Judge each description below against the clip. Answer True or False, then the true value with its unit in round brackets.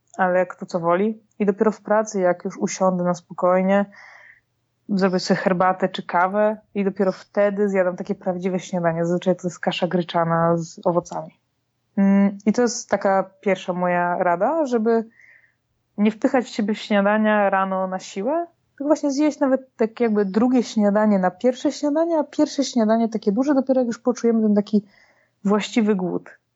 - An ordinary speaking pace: False (165 wpm)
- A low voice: False (205 Hz)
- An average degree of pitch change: True (3.7 semitones)